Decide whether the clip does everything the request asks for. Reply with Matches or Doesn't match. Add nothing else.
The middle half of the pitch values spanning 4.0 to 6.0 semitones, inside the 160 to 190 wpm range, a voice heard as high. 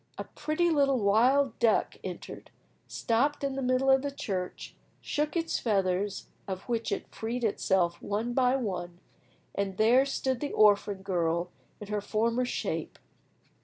Doesn't match